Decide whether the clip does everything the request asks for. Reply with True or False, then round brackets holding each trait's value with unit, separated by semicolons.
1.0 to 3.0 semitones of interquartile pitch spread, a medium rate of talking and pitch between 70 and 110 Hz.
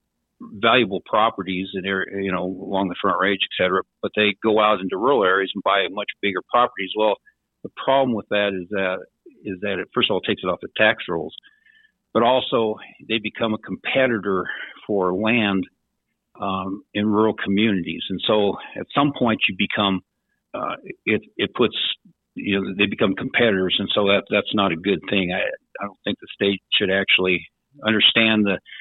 True (2.6 semitones; 180 wpm; 100 Hz)